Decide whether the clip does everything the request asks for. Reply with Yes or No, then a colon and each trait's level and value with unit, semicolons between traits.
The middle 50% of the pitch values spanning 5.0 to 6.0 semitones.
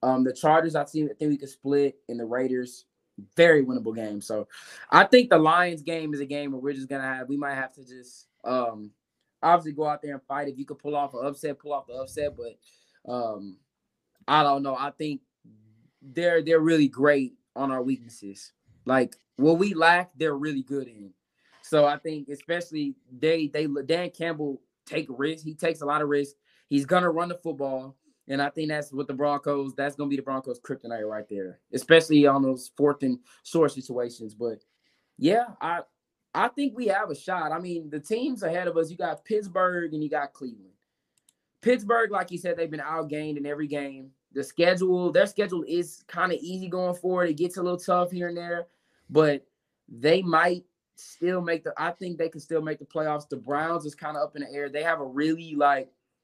No: average, 3.7 semitones